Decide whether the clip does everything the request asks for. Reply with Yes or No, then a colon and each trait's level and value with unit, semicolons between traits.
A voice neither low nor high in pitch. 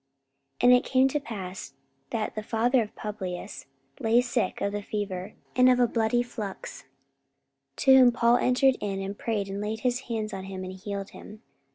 No: high, 220 Hz